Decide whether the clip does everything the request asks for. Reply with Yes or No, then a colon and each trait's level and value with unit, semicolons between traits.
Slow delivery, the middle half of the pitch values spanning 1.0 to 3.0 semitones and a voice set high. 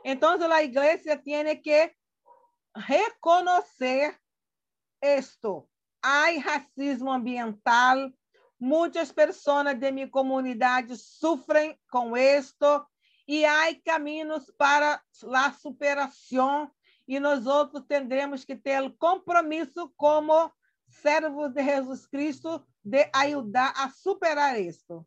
Yes: slow, 100 wpm; narrow, 2.6 semitones; very high, 290 Hz